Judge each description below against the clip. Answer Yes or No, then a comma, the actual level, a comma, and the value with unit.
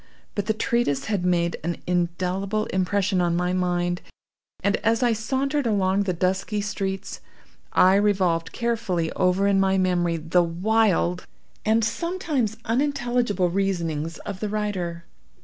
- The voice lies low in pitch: No, high, 195 Hz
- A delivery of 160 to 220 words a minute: No, slow, 135 wpm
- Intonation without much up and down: No, average, 3.6 semitones